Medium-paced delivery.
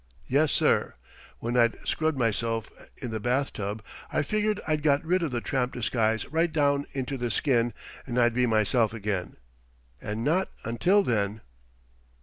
Yes: average, 155 wpm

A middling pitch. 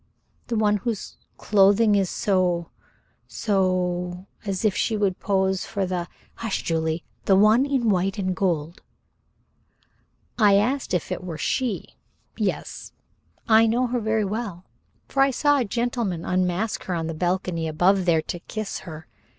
No: high, 195 Hz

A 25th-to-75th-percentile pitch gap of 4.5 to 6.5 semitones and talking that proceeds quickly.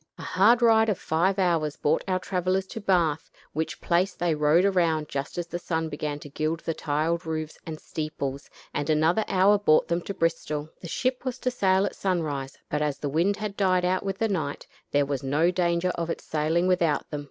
No: average, 3.6 semitones; fast, 210 wpm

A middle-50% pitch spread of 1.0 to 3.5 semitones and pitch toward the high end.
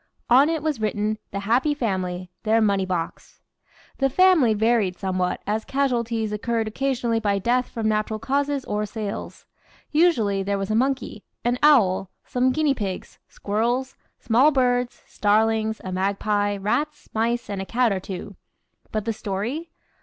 No: average, 4.0 semitones; high, 220 Hz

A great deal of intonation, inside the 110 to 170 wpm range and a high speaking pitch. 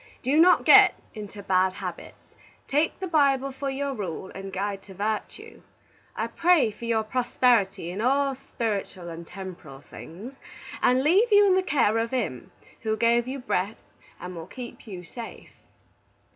Yes: wide, 5.9 semitones; average, 160 wpm; high, 230 Hz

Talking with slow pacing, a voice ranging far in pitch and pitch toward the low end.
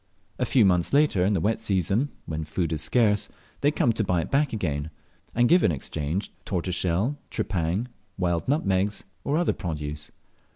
No: average, 170 wpm; wide, 6.0 semitones; very low, 95 Hz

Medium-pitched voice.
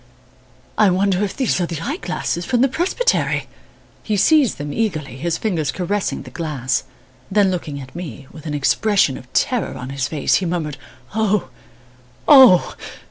Yes: medium, 180 Hz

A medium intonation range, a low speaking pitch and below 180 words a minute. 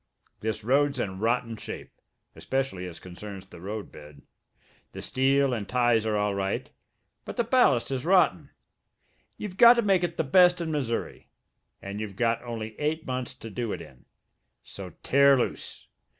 No: wide, 5.7 semitones; low, 120 Hz; average, 165 wpm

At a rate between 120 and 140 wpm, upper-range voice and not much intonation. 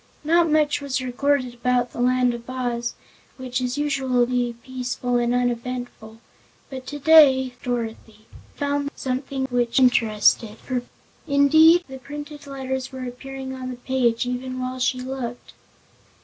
Yes: slow, 135 wpm; very high, 255 Hz; narrow, 1.9 semitones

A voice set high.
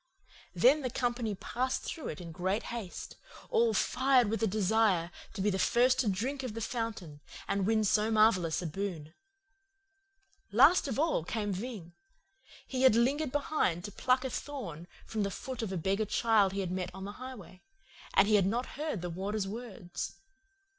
Yes: high, 215 Hz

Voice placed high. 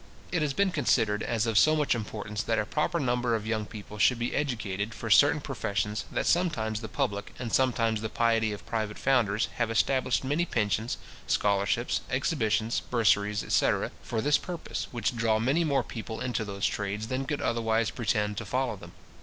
No: low, 115 Hz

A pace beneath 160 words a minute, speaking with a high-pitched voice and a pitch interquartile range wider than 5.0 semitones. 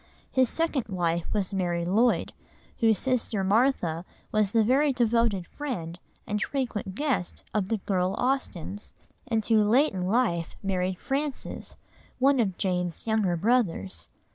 Yes: average, 140 wpm; high, 210 Hz; wide, 5.5 semitones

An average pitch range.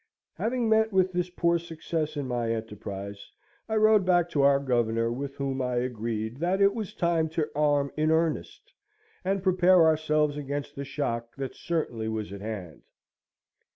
No: wide, 6.5 semitones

